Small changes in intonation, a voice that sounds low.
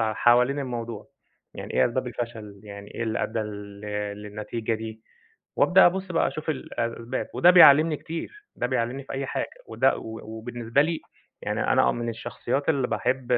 No: average, 3.8 semitones; low, 120 Hz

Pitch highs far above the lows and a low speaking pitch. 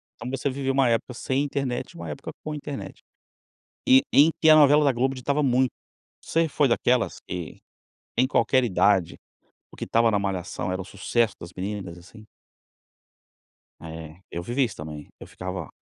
Yes: wide, 6.6 semitones; low, 120 Hz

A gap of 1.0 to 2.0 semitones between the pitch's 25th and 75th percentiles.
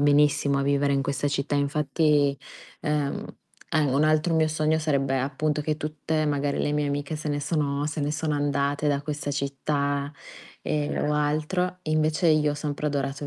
Yes: narrow, 1.3 semitones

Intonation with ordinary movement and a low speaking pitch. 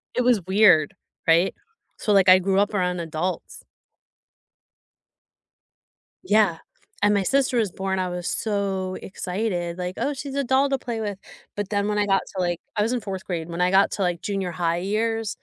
No: average, 3.1 semitones; high, 195 Hz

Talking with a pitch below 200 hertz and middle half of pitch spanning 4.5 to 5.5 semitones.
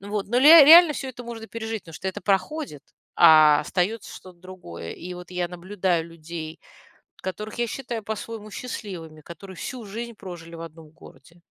Yes: high, 190 Hz; average, 5.1 semitones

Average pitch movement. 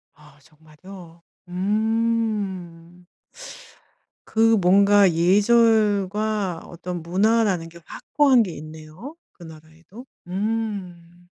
Yes: average, 4.3 semitones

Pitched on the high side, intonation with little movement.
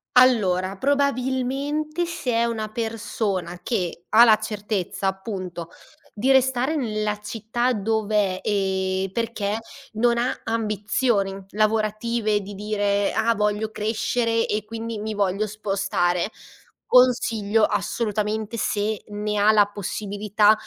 Yes: high, 215 Hz; narrow, 2.3 semitones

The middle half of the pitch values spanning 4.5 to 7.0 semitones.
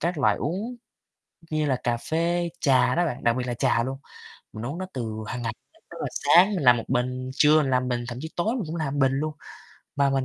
Yes: average, 4.9 semitones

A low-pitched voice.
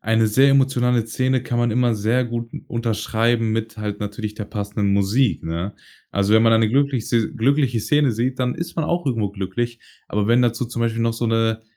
Yes: low, 115 Hz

